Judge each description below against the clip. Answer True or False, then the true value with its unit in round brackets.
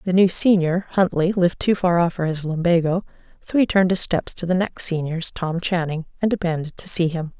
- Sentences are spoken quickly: True (220 wpm)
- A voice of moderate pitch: True (175 Hz)